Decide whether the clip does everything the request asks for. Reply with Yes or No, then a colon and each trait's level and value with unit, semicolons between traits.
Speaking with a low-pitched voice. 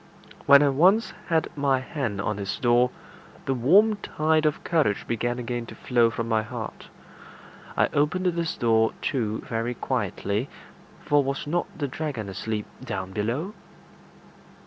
Yes: low, 130 Hz